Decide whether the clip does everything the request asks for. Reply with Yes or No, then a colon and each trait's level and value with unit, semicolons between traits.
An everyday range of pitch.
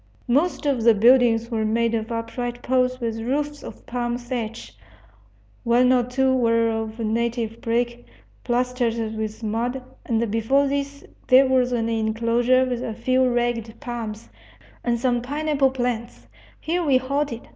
No: narrow, 2.1 semitones